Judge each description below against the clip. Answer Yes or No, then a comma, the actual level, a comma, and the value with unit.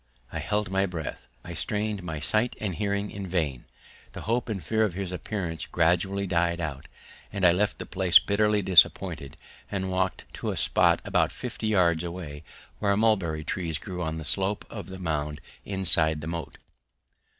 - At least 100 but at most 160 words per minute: No, average, 175 wpm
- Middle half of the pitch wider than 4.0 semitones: No, average, 3.6 semitones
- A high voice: No, very low, 90 Hz